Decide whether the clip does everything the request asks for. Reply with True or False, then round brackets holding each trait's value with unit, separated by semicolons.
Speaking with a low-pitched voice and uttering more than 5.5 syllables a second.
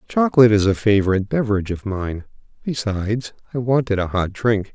True (110 Hz; 6.3 syllables/s)